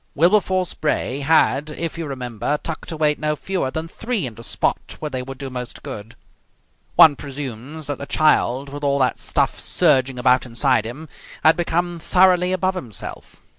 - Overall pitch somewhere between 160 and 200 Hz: No, medium, 145 Hz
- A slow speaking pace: No, average, 170 wpm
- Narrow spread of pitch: No, average, 4.2 semitones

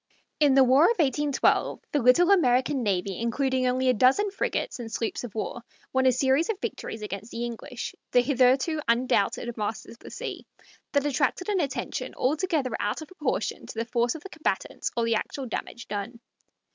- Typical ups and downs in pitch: Yes, average, 3.9 semitones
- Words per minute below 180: No, average, 185 wpm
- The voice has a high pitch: Yes, very high, 255 Hz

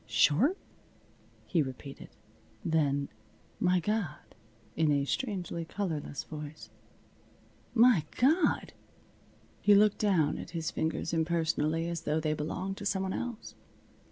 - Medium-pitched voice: Yes, medium, 165 Hz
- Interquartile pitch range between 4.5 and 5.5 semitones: Yes, average, 4.8 semitones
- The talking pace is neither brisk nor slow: No, slow, 120 wpm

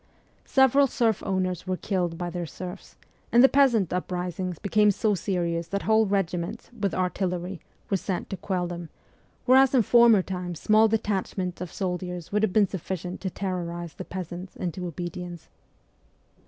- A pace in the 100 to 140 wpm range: No, average, 155 wpm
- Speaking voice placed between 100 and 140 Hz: No, medium, 185 Hz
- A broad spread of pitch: No, average, 2.9 semitones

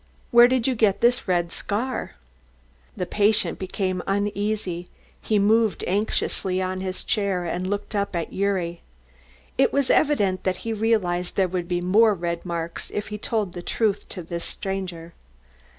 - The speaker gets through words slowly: No, average, 160 wpm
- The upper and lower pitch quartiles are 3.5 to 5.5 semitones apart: No, average, 3.1 semitones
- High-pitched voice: Yes, high, 195 Hz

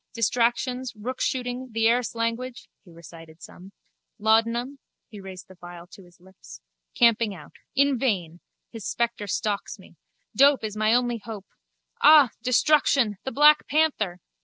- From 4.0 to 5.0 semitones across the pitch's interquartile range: Yes, average, 4.5 semitones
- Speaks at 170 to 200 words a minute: No, average, 140 wpm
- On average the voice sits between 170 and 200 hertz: No, high, 230 Hz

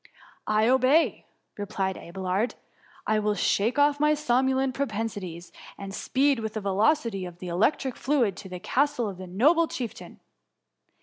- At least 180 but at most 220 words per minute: No, average, 165 wpm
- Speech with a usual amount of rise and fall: No, wide, 5.7 semitones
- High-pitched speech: Yes, high, 220 Hz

